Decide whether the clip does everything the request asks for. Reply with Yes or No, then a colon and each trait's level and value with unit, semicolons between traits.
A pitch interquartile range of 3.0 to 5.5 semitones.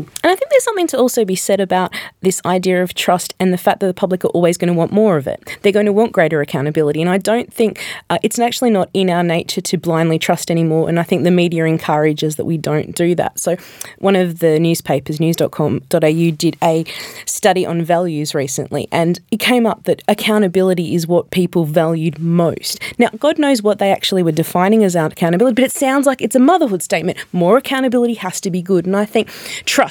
Yes: average, 4.0 semitones